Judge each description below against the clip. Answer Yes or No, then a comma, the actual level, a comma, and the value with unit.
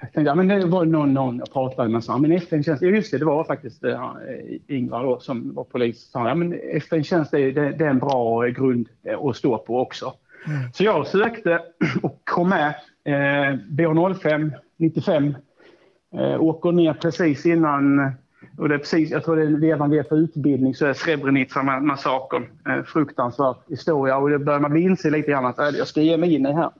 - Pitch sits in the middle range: Yes, medium, 150 Hz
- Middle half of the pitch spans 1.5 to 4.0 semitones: Yes, average, 3.3 semitones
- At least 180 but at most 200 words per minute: Yes, average, 190 wpm